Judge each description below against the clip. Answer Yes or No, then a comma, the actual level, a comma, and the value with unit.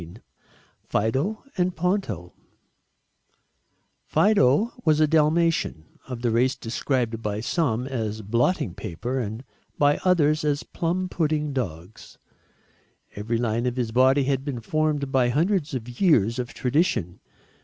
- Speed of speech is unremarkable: No, slow, 130 wpm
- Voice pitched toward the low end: Yes, low, 130 Hz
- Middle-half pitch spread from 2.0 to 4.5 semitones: No, average, 5.3 semitones